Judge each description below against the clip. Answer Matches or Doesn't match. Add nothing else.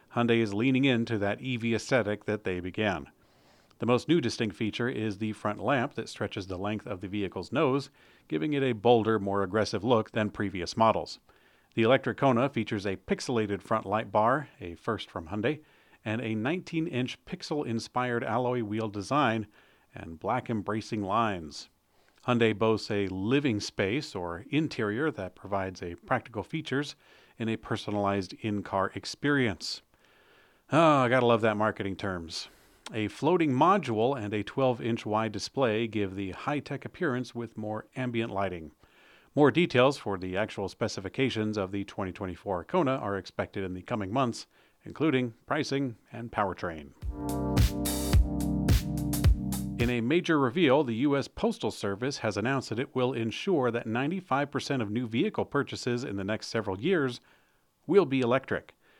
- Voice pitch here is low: Matches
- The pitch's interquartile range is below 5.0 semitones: Matches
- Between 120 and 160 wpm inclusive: Matches